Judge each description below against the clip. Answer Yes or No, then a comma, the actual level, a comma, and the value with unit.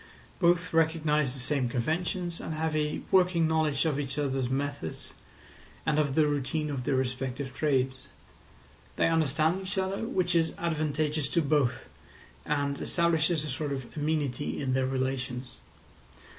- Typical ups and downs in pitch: Yes, average, 3.3 semitones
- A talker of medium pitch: Yes, medium, 150 Hz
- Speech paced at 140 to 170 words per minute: Yes, average, 145 wpm